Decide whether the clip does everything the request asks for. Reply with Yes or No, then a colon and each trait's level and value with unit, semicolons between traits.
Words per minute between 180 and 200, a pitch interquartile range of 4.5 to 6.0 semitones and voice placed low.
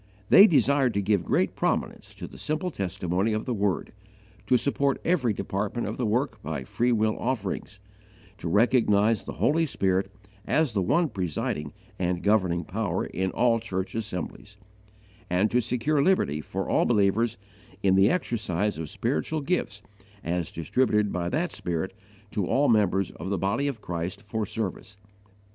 No: average, 160 wpm; average, 4.8 semitones; low, 105 Hz